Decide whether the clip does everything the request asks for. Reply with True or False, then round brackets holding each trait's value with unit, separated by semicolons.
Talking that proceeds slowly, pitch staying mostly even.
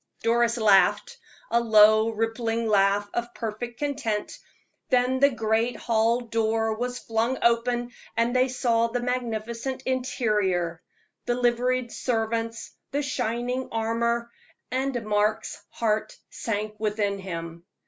True (115 wpm; 2.0 semitones)